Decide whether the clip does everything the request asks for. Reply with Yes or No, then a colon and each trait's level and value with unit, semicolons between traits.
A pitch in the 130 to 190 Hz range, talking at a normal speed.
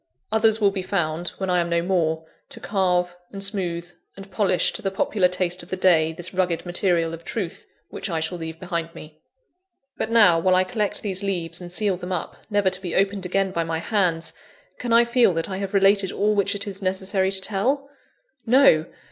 No: medium, 185 Hz; fast, 210 wpm